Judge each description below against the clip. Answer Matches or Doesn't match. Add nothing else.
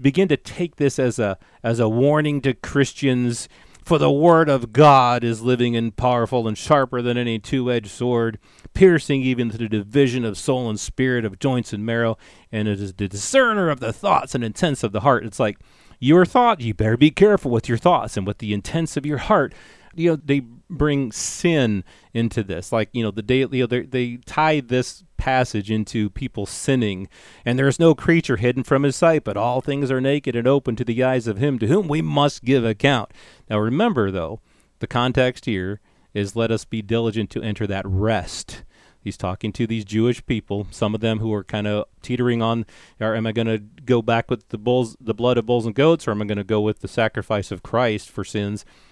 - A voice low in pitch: Matches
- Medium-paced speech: Doesn't match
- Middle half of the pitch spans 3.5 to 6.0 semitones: Matches